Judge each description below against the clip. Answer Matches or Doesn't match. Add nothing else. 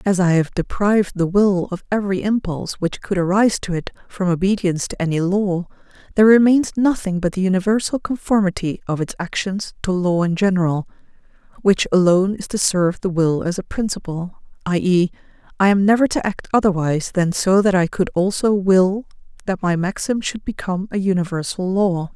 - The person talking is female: Matches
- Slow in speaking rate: Doesn't match